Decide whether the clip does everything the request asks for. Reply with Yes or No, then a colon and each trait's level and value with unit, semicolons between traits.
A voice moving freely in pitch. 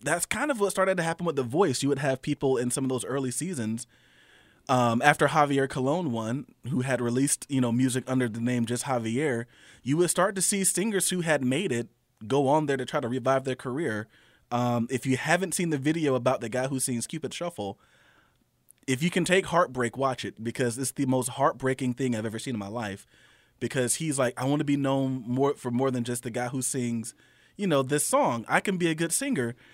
No: average, 3.7 semitones